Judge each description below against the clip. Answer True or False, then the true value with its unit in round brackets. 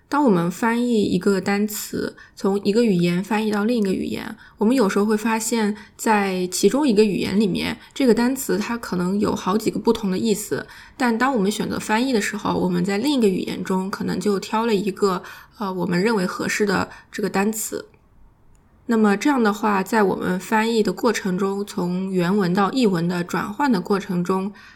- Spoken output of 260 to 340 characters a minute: True (295 characters per minute)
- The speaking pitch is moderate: False (205 Hz)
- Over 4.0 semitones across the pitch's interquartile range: False (2.7 semitones)